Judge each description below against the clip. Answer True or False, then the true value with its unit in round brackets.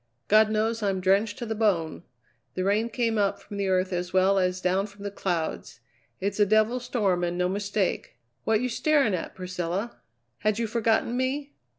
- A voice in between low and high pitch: False (205 Hz)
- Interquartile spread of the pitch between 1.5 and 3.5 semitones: True (3.1 semitones)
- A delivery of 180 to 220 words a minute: True (190 wpm)